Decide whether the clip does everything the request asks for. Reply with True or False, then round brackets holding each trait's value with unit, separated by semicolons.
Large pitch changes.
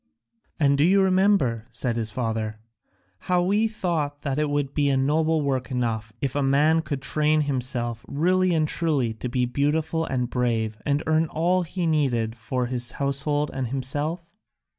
False (4.3 semitones)